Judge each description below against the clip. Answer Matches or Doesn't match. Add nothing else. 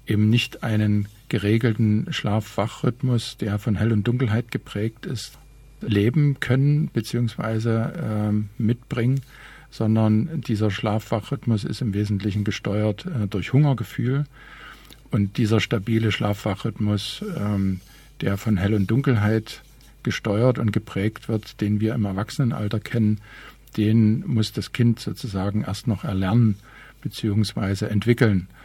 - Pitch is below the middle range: Matches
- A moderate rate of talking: Doesn't match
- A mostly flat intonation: Matches